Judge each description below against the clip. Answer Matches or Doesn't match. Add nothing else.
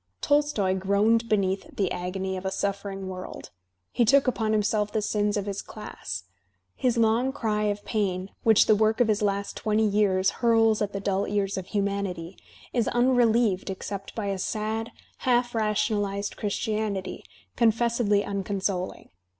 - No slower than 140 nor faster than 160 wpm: Matches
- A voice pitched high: Matches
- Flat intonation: Matches